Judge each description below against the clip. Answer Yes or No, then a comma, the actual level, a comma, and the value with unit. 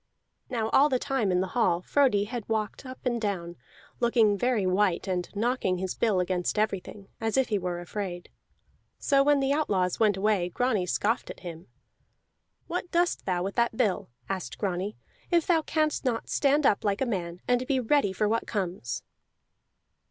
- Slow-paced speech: No, average, 180 wpm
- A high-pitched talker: Yes, high, 210 Hz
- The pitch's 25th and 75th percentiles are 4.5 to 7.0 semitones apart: Yes, wide, 5.4 semitones